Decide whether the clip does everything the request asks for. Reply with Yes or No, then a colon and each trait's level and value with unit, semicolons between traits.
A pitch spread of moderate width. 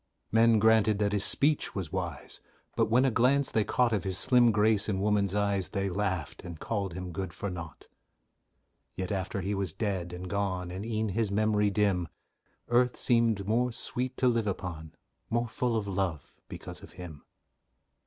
Yes: average, 3.3 semitones